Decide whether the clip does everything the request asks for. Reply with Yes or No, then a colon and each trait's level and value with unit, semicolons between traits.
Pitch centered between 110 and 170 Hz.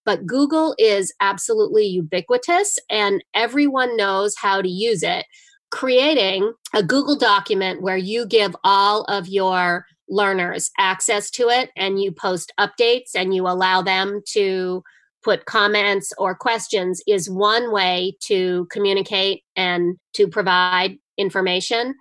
No: high, 200 Hz